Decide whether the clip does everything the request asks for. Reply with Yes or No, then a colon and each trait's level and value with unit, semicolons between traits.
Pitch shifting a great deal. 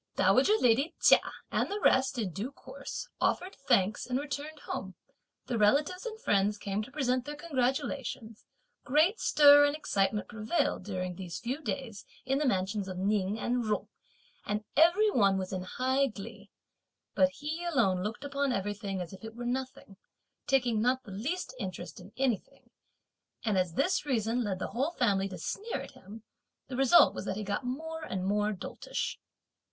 Yes: wide, 6.0 semitones